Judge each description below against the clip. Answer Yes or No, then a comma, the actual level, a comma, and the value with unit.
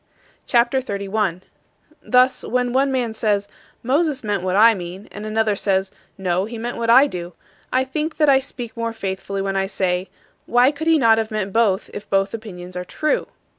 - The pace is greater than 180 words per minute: Yes, average, 195 wpm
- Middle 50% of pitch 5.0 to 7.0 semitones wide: No, average, 4.5 semitones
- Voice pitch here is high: Yes, high, 220 Hz